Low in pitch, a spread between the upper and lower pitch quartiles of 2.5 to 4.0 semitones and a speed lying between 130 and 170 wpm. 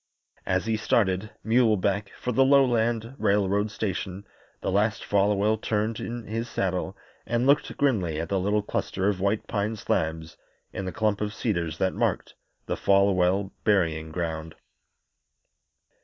Yes: low, 100 Hz; average, 3.0 semitones; average, 140 wpm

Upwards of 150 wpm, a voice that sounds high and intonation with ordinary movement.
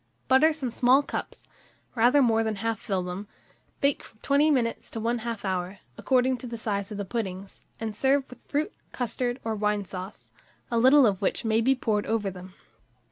Yes: average, 190 wpm; high, 225 Hz; average, 4.1 semitones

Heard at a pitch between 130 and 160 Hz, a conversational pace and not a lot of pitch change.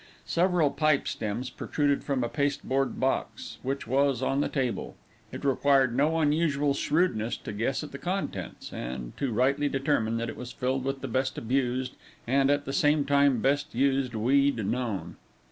Yes: low, 135 Hz; average, 170 wpm; narrow, 2.3 semitones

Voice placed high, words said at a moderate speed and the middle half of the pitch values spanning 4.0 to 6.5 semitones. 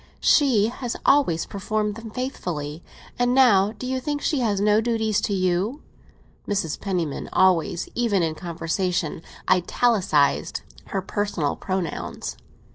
No: high, 200 Hz; slow, 125 wpm; average, 5.1 semitones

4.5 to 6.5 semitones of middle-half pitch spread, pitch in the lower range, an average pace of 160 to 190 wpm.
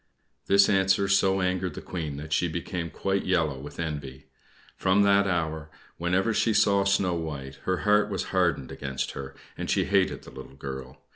Yes: average, 5.0 semitones; very low, 90 Hz; average, 175 wpm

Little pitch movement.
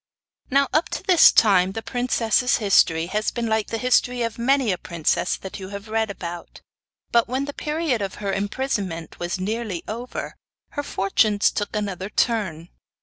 No: average, 4.2 semitones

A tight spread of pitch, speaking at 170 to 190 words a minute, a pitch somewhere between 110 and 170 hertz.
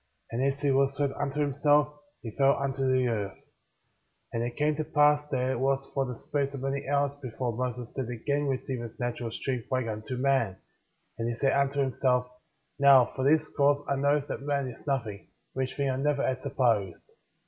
No: narrow, 2.2 semitones; fast, 205 wpm; low, 135 Hz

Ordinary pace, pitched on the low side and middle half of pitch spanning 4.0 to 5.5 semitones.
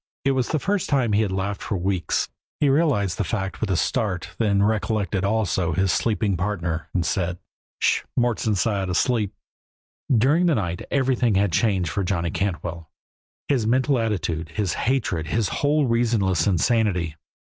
Yes: average, 165 wpm; low, 100 Hz; average, 4.6 semitones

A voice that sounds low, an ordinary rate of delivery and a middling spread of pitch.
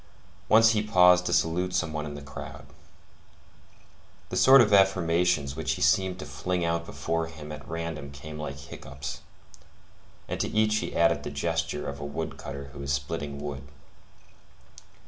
Yes: very low, 80 Hz; average, 165 wpm; average, 4.0 semitones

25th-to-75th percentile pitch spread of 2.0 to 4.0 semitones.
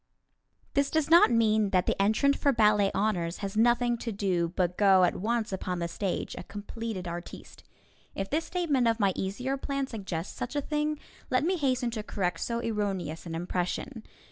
No: average, 5.3 semitones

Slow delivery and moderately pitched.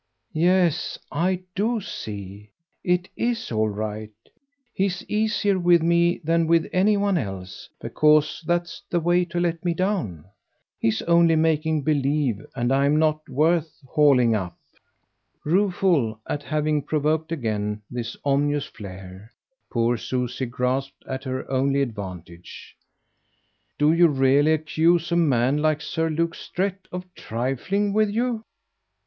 Yes: slow, 130 wpm; medium, 155 Hz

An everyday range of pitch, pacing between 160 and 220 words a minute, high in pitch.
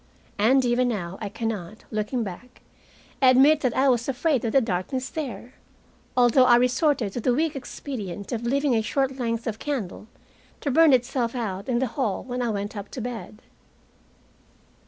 Yes: average, 3.3 semitones; average, 180 wpm; high, 245 Hz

